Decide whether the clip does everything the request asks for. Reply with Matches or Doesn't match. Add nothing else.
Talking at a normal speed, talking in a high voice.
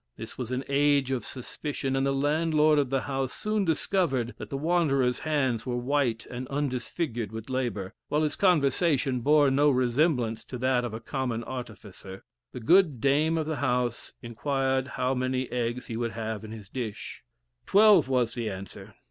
Doesn't match